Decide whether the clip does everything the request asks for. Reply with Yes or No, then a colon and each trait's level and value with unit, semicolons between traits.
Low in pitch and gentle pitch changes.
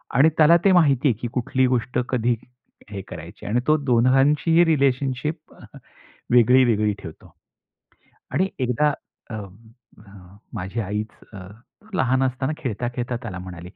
No: low, 125 Hz; average, 4.6 semitones